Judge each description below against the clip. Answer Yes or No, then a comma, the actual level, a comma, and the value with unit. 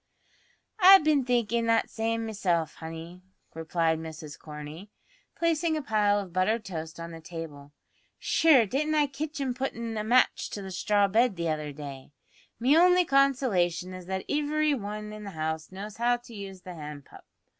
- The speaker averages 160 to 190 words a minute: Yes, average, 175 wpm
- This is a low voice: No, high, 205 Hz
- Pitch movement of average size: No, wide, 7.4 semitones